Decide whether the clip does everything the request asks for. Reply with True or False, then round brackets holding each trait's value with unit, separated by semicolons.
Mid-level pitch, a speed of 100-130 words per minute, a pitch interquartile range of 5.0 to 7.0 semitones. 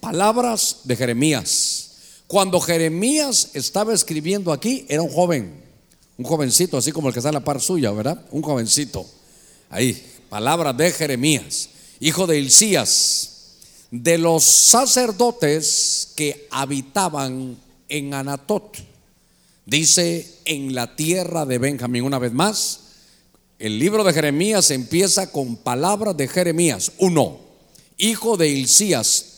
True (155 Hz; 125 wpm; 5.4 semitones)